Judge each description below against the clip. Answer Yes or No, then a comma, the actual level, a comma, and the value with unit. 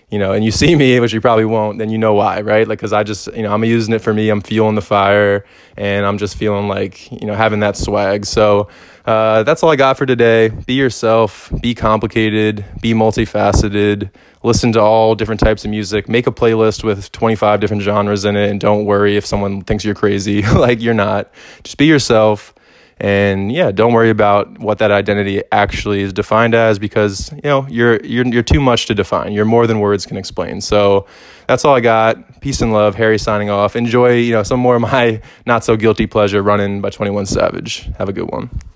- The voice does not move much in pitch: Yes, narrow, 1.9 semitones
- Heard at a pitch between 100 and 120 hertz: Yes, low, 110 Hz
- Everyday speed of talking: No, fast, 220 wpm